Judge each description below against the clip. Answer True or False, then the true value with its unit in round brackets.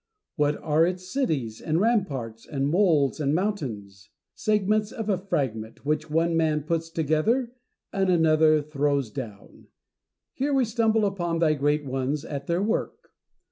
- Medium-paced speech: True (150 wpm)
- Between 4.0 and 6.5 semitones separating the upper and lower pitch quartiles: True (5.5 semitones)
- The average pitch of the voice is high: False (155 Hz)